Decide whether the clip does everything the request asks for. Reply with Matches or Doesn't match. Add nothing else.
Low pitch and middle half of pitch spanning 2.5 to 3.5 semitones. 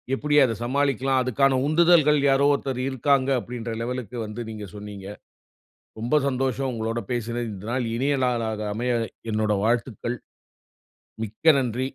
Matches